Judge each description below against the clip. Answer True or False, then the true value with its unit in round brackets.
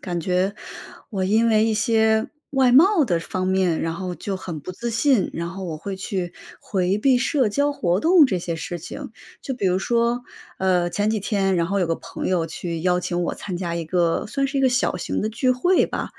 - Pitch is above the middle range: True (195 Hz)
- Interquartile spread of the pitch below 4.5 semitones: False (5.0 semitones)